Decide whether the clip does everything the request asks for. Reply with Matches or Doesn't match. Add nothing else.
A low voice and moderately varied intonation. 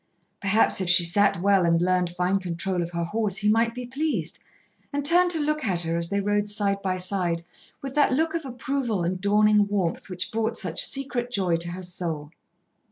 Doesn't match